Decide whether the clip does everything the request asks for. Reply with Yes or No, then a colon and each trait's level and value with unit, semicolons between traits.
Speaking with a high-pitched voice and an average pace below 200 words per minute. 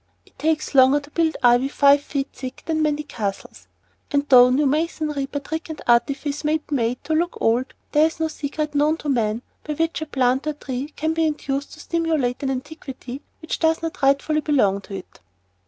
No: very high, 290 Hz; fast, 205 wpm